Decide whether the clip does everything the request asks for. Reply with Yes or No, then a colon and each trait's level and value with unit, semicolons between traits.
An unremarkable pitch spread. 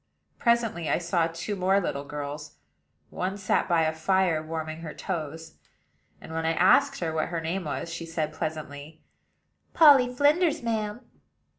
Yes: average, 3.9 semitones